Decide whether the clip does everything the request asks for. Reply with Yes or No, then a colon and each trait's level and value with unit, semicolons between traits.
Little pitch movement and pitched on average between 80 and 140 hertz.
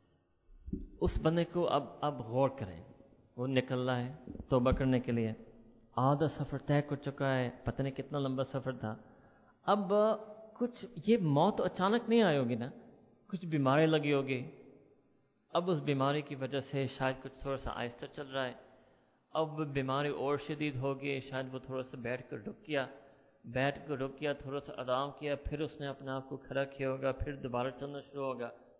Yes: narrow, 2.1 semitones; low, 135 Hz